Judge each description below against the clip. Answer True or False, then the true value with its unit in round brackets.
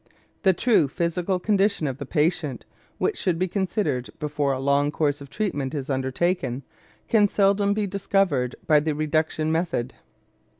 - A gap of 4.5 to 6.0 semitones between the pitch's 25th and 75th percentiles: True (5.3 semitones)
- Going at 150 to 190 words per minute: True (155 wpm)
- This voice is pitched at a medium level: True (160 Hz)